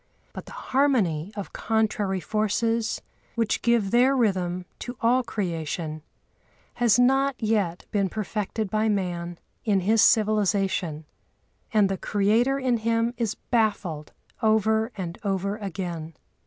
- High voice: Yes, high, 210 Hz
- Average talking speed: No, slow, 125 wpm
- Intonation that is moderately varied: Yes, average, 3.4 semitones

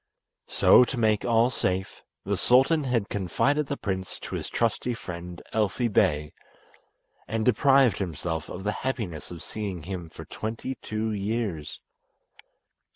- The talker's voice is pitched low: Yes, low, 105 Hz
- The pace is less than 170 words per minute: Yes, average, 140 wpm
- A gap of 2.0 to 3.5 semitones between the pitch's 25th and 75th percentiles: No, average, 4.9 semitones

